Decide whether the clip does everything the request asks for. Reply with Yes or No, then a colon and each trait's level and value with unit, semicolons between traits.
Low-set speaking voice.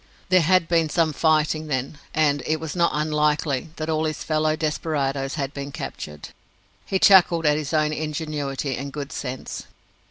No: medium, 155 Hz